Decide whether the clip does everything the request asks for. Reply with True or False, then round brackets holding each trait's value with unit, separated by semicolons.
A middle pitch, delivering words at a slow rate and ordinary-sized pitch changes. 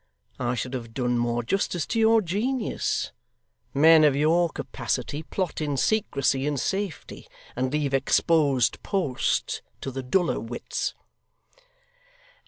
False (145 Hz; 125 wpm; 5.7 semitones)